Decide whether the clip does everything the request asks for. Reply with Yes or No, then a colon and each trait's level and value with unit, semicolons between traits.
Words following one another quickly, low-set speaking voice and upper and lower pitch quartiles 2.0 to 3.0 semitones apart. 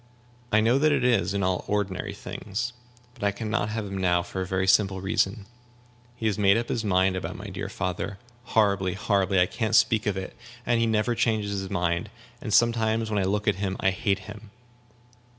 Yes: fast, 210 wpm; low, 100 Hz; average, 2.7 semitones